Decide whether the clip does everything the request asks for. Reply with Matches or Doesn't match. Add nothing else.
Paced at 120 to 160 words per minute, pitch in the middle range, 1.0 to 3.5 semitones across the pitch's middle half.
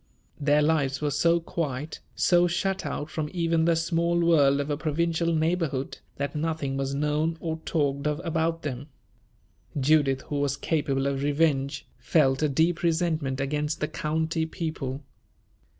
Matches